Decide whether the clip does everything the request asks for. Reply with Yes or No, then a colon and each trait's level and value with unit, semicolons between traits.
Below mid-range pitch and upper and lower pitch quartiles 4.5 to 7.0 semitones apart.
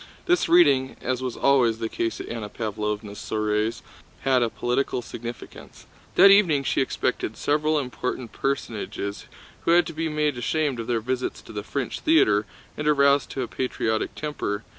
Yes: low, 130 Hz; average, 4.8 semitones